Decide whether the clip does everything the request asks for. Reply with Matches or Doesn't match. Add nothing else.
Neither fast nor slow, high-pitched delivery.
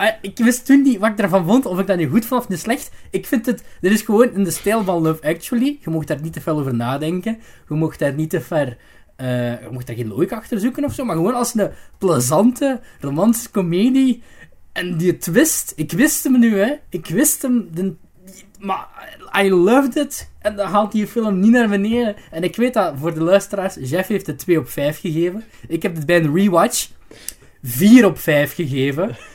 Doesn't match